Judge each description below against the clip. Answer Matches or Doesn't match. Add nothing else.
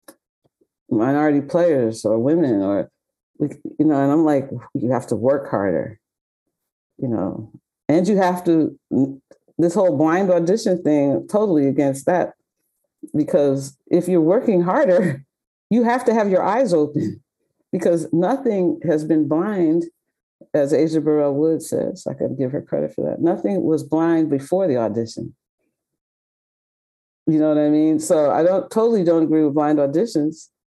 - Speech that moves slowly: Doesn't match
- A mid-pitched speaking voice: Matches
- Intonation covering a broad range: Doesn't match